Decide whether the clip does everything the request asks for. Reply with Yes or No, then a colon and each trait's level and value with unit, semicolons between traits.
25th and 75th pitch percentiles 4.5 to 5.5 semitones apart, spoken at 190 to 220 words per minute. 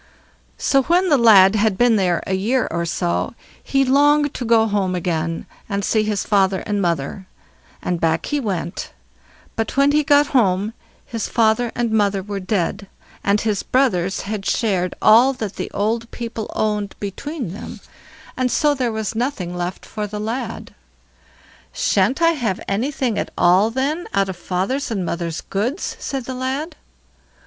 No: average, 5.1 semitones; average, 165 wpm